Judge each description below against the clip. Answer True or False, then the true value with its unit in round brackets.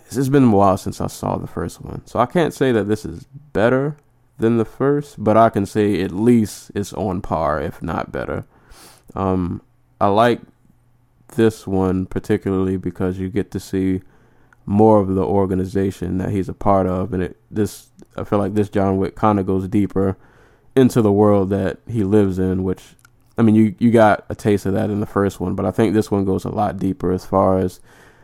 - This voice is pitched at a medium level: False (100 Hz)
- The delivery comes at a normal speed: False (210 wpm)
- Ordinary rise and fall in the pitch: True (3.0 semitones)